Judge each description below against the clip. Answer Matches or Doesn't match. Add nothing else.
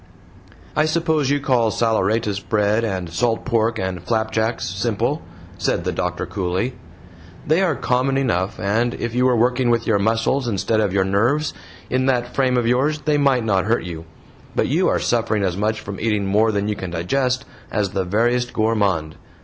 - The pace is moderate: Matches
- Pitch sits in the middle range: Doesn't match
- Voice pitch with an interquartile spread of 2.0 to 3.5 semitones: Doesn't match